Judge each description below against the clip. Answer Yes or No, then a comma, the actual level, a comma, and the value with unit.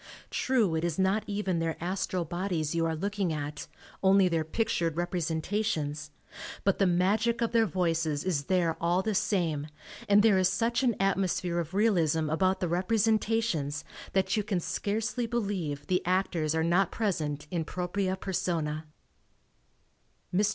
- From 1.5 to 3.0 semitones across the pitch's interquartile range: No, average, 3.8 semitones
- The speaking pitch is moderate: Yes, medium, 180 Hz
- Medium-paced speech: Yes, average, 150 wpm